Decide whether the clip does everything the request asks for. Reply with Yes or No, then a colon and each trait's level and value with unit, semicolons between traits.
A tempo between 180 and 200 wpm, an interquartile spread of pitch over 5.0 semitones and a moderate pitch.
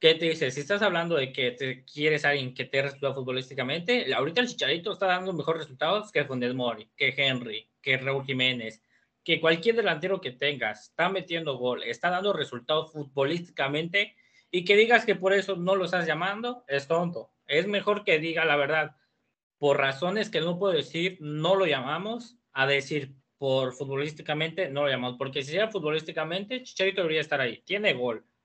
Yes: average, 185 wpm; wide, 5.6 semitones; medium, 155 Hz